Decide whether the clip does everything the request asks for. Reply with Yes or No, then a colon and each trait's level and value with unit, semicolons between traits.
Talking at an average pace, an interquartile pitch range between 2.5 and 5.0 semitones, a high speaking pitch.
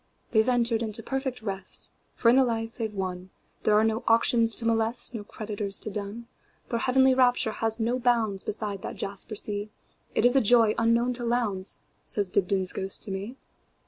Yes: average, 165 wpm; average, 2.8 semitones; high, 225 Hz